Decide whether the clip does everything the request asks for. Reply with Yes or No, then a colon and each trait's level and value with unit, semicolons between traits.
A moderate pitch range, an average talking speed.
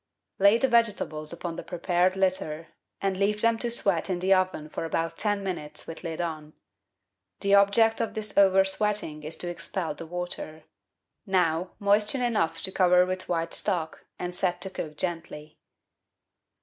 Yes: average, 3.5 semitones; average, 165 wpm